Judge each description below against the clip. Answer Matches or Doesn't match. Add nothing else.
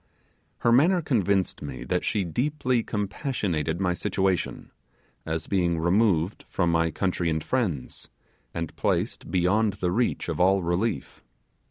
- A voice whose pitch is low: Matches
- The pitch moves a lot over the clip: Doesn't match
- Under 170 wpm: Matches